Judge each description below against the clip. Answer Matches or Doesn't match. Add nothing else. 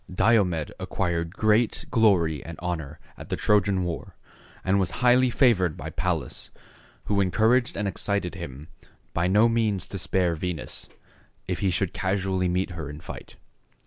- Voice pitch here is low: Matches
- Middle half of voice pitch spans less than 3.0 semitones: Doesn't match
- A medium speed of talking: Matches